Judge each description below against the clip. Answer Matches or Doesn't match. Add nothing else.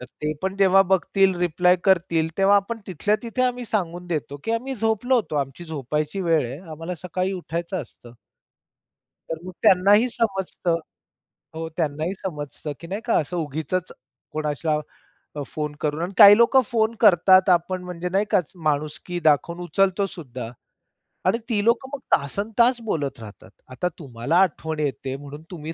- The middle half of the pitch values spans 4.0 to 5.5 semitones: Matches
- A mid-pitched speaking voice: Matches